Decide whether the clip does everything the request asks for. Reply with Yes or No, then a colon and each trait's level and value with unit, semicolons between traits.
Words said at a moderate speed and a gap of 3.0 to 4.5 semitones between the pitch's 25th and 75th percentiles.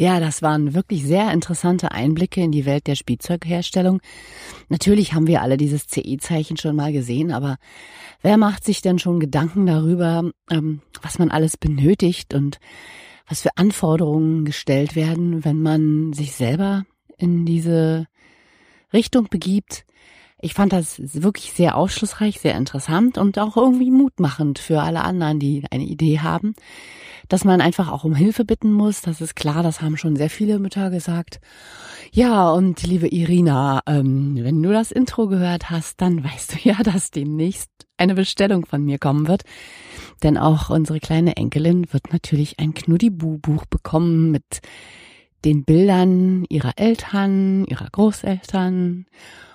Yes: average, 150 wpm; average, 3.8 semitones